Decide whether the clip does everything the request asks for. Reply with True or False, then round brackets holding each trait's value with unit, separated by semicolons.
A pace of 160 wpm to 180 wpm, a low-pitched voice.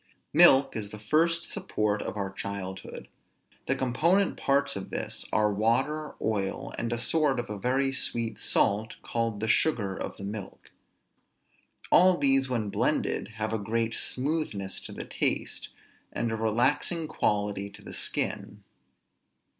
False (145 wpm; 115 Hz)